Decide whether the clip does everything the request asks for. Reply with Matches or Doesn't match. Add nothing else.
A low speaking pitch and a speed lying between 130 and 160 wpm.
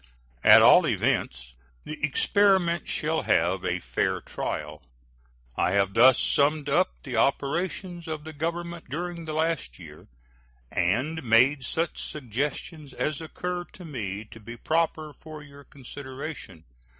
Doesn't match